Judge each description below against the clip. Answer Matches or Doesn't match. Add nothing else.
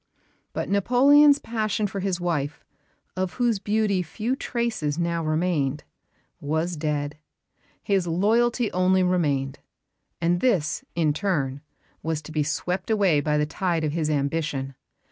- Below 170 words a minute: Matches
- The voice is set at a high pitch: Doesn't match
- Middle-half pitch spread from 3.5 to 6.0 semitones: Matches